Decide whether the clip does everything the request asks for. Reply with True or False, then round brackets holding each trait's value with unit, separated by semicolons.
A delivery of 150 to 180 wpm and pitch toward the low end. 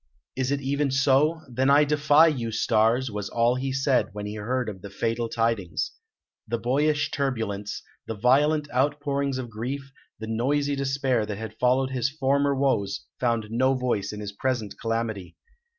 True (165 wpm; 125 Hz)